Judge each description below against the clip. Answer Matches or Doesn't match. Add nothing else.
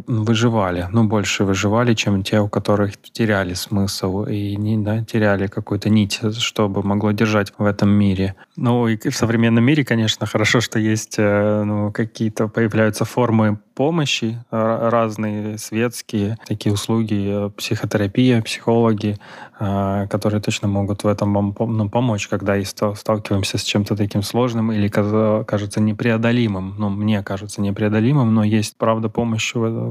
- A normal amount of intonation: Doesn't match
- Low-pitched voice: Matches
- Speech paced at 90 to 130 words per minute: Doesn't match